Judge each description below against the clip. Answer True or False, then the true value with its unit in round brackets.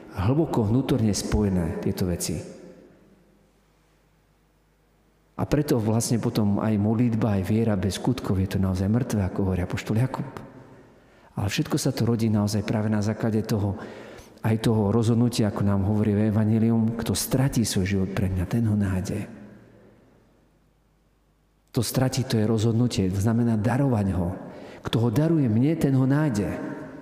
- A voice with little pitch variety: False (3.5 semitones)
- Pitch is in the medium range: False (110 Hz)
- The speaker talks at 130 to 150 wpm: True (145 wpm)